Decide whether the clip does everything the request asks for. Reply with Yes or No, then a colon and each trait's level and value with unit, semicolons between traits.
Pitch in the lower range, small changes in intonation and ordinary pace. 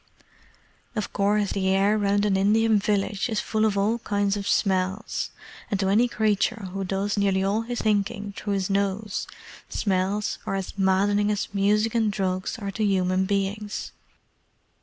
No: high, 200 Hz; narrow, 1.5 semitones; average, 160 wpm